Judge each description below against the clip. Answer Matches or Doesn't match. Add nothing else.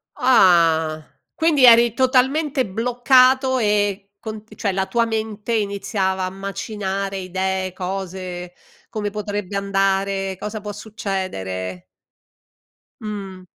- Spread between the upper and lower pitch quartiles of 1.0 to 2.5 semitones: Doesn't match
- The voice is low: Doesn't match